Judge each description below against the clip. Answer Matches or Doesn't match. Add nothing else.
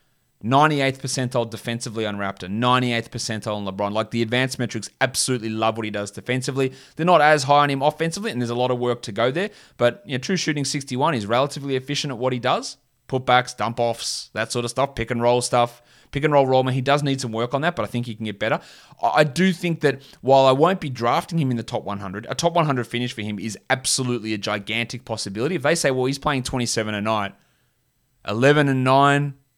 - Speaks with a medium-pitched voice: Doesn't match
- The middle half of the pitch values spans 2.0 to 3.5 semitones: Matches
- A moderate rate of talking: Doesn't match